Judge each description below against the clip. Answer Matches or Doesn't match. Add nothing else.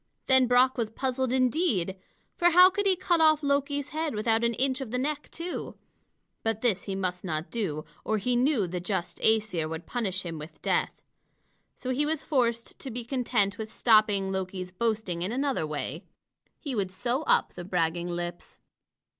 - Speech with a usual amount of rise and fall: Doesn't match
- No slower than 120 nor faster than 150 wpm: Doesn't match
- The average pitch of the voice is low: Doesn't match